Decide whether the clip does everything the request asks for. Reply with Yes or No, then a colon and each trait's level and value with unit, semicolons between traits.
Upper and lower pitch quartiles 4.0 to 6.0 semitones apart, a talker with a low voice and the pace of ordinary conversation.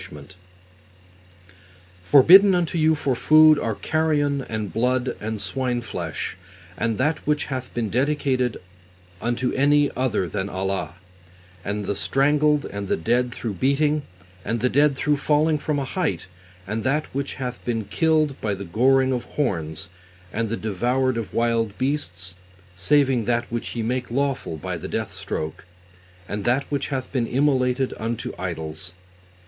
Yes: average, 4.8 semitones; low, 125 Hz; average, 150 wpm